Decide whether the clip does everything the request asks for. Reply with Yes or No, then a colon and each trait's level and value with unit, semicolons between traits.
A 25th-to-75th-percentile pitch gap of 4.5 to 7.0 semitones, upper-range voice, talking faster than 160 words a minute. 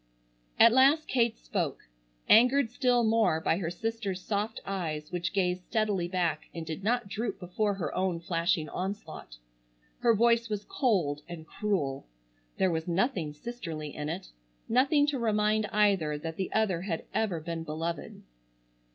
No: average, 5.1 semitones; high, 195 Hz; average, 150 wpm